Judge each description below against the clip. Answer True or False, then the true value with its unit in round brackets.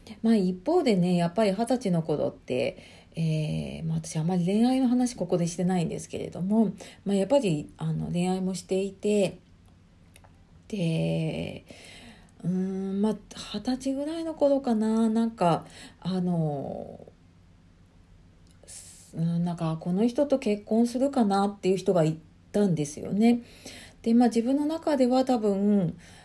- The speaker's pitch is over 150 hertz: True (185 Hz)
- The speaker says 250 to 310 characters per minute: True (270 characters per minute)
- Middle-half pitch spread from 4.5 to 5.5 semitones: False (6.3 semitones)